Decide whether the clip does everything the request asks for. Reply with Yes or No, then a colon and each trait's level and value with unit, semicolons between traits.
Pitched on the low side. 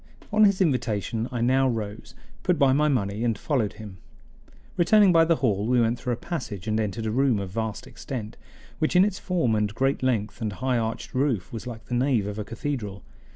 Yes: low, 120 Hz